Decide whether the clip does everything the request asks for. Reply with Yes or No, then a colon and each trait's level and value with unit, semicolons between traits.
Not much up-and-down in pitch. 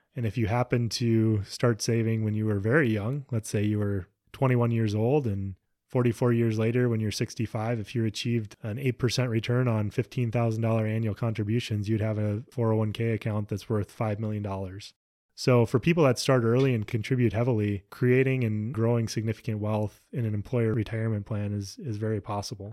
Yes: narrow, 2.2 semitones